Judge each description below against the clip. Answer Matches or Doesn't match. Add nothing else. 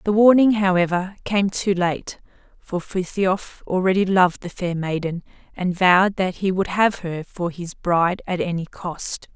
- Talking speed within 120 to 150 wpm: Doesn't match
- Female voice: Matches